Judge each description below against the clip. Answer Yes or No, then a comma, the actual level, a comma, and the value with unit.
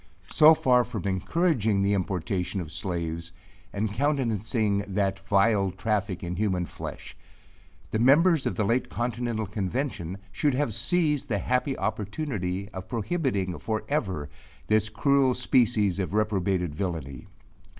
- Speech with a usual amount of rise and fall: Yes, average, 4.9 semitones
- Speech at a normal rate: No, slow, 130 wpm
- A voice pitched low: Yes, low, 105 Hz